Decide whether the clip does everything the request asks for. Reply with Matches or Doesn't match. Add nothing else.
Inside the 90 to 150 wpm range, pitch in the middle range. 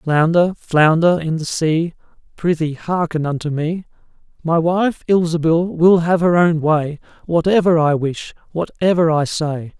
Matches